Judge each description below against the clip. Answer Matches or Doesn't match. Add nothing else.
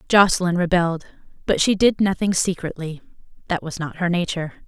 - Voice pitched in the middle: Matches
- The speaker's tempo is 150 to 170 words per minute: Matches